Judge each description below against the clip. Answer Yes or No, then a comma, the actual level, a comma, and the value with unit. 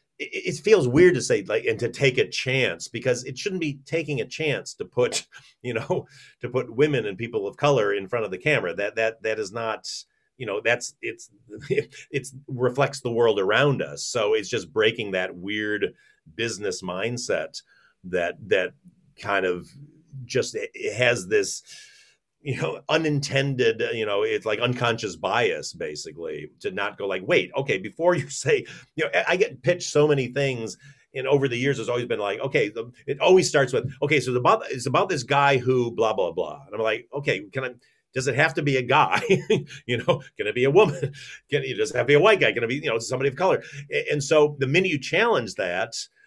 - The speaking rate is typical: No, fast, 210 wpm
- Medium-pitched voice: Yes, medium, 155 Hz